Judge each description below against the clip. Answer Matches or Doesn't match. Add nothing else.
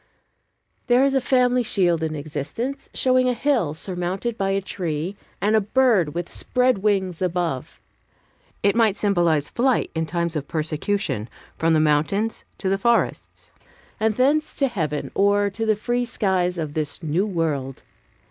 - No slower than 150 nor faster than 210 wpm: Matches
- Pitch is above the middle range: Matches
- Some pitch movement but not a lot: Doesn't match